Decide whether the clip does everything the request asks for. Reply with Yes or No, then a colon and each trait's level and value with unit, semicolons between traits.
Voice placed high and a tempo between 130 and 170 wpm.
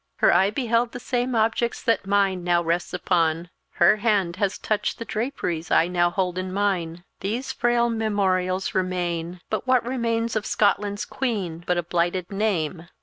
Yes: high, 195 Hz; average, 165 wpm